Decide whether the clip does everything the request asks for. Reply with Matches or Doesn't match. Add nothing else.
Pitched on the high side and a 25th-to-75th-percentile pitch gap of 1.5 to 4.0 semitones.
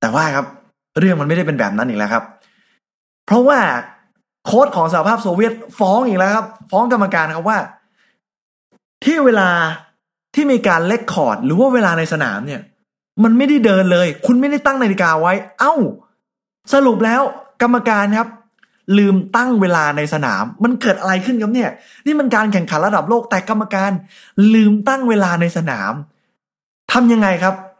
Doesn't match